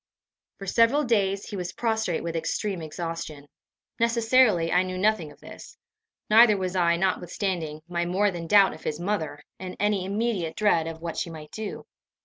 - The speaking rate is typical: Yes, average, 170 wpm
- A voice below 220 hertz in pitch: Yes, medium, 185 Hz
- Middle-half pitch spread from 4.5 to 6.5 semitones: No, average, 4.0 semitones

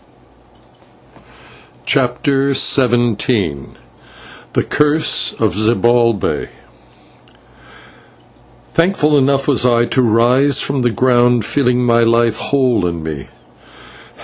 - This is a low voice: Yes, low, 120 Hz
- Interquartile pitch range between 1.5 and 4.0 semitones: Yes, average, 2.8 semitones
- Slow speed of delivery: Yes, slow, 90 wpm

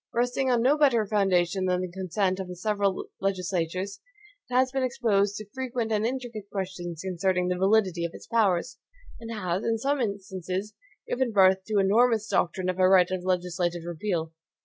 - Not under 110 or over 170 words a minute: No, average, 180 wpm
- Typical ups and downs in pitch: Yes, average, 3.7 semitones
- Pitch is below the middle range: No, high, 195 Hz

